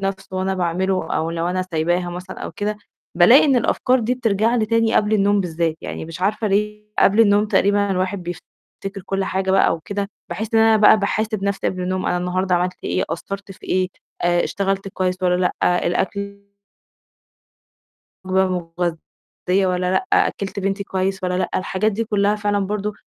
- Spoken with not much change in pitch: Yes, narrow, 2.2 semitones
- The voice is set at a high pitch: Yes, high, 195 Hz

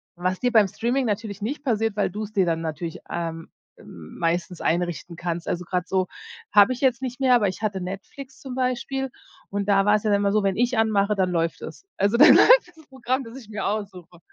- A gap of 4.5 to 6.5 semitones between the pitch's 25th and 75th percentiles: Yes, average, 5.2 semitones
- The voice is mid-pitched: No, high, 205 Hz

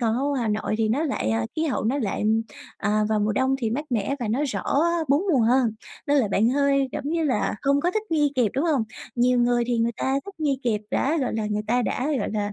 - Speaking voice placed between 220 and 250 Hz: Yes, high, 245 Hz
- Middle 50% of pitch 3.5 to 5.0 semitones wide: Yes, average, 4.4 semitones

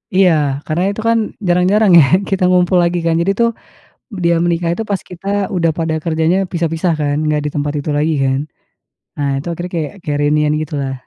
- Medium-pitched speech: Yes, medium, 165 Hz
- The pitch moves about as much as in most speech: Yes, average, 3.2 semitones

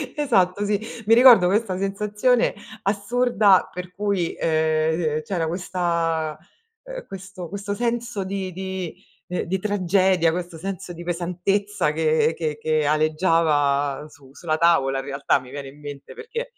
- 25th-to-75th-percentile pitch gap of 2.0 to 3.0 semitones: No, average, 4.2 semitones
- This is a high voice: No, medium, 180 Hz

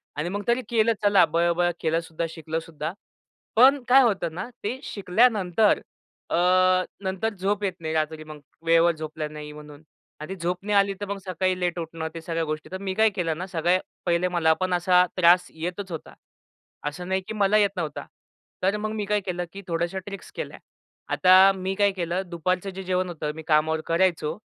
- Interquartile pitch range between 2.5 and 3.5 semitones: Yes, average, 3.2 semitones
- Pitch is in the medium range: Yes, medium, 180 Hz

